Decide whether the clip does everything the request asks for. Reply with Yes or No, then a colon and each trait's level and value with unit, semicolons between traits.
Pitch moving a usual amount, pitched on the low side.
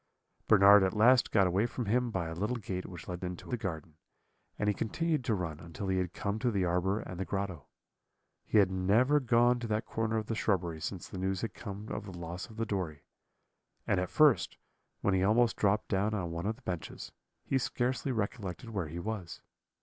Yes: average, 3.7 semitones; low, 100 Hz